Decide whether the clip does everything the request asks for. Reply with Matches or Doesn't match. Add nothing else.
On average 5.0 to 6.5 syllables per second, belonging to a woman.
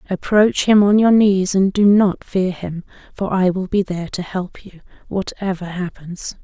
Doesn't match